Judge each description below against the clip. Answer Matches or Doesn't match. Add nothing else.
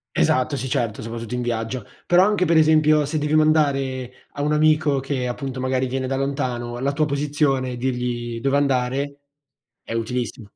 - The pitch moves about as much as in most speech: Matches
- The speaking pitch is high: Doesn't match